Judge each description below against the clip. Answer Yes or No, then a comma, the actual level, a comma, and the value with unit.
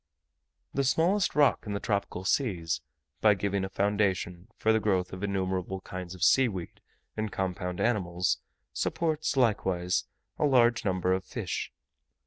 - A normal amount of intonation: Yes, average, 3.7 semitones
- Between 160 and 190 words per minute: No, average, 145 wpm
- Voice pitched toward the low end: Yes, low, 100 Hz